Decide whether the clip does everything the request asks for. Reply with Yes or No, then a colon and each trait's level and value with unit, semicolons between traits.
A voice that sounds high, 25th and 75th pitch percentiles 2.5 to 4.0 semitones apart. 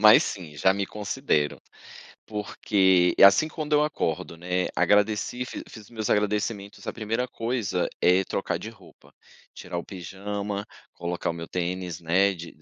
No: low, 100 Hz; average, 3.2 semitones